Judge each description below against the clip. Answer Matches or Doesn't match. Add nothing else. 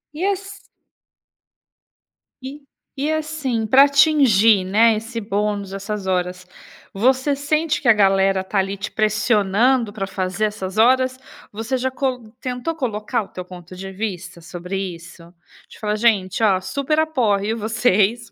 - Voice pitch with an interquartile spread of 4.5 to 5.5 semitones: Matches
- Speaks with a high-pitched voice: Matches